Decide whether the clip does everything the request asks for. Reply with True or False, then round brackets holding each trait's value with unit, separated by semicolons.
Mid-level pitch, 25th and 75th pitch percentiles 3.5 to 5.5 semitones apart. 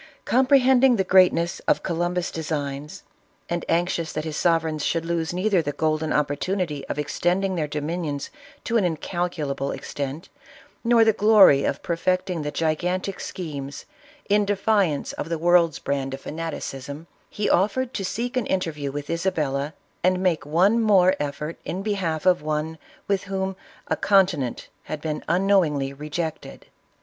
True (170 Hz; 4.2 semitones)